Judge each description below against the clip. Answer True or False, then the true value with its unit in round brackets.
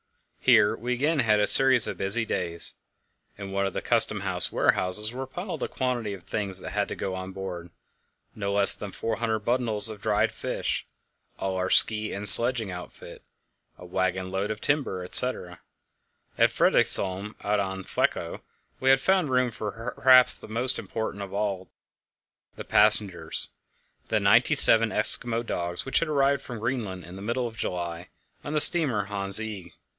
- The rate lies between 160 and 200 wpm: True (170 wpm)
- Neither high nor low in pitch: False (105 Hz)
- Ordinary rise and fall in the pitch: True (4.2 semitones)